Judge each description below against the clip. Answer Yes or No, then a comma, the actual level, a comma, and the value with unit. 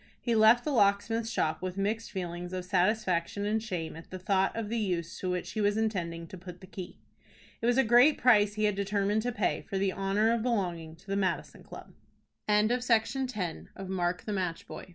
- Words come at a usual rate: No, fast, 215 wpm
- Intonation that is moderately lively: Yes, average, 3.4 semitones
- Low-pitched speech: No, high, 200 Hz